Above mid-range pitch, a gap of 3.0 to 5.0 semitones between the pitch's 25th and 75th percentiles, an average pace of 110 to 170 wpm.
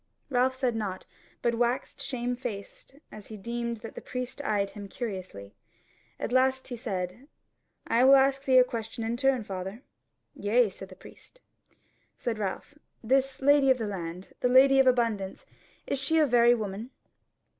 Yes: high, 240 Hz; average, 4.1 semitones; average, 165 wpm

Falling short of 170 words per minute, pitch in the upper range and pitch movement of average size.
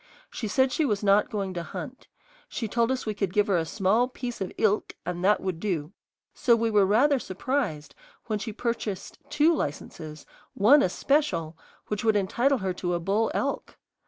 No: average, 190 wpm; high, 210 Hz; average, 4.4 semitones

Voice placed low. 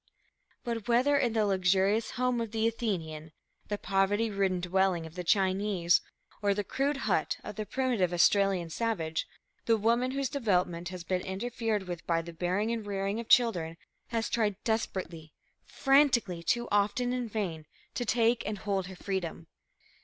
No: high, 205 Hz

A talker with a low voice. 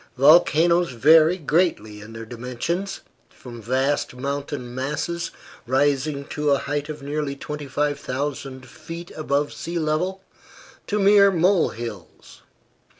No: medium, 145 Hz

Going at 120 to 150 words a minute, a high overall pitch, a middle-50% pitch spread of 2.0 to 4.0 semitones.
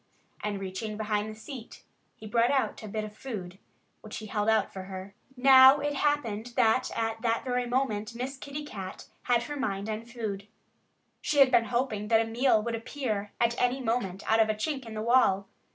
No: average, 200 wpm; high, 225 Hz; average, 3.1 semitones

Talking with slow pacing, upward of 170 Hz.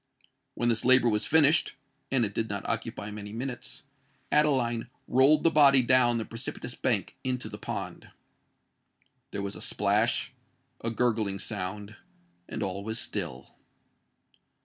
No: slow, 125 wpm; low, 120 Hz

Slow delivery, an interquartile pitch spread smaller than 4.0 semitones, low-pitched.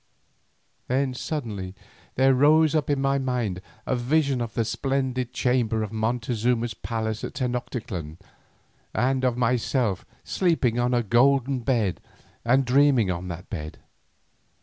Yes: slow, 130 wpm; average, 3.2 semitones; low, 125 Hz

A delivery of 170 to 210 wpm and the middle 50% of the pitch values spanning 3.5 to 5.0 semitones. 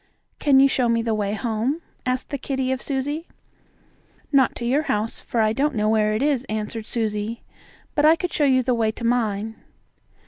Yes: average, 200 wpm; average, 3.9 semitones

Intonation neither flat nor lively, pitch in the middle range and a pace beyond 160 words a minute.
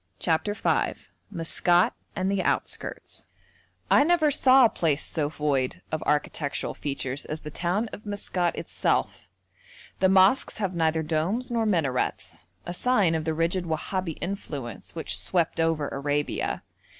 No: average, 4.5 semitones; medium, 165 Hz; average, 145 wpm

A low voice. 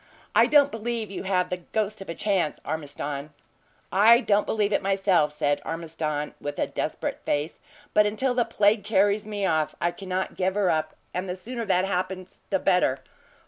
No: high, 190 Hz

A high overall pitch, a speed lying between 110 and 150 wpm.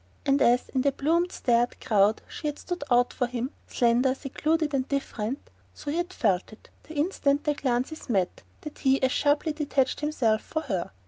No: very high, 275 Hz; average, 185 wpm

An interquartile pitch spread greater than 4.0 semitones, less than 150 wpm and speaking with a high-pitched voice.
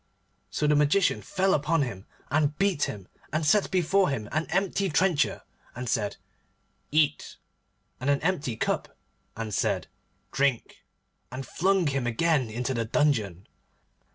No: wide, 5.6 semitones; average, 140 wpm; medium, 145 Hz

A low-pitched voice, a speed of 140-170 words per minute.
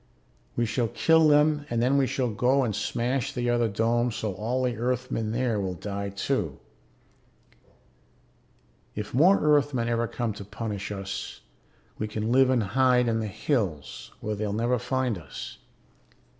Yes: low, 120 Hz; average, 155 wpm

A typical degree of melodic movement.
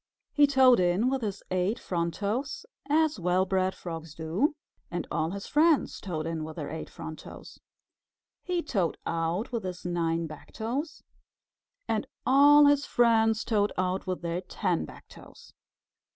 No: wide, 7.2 semitones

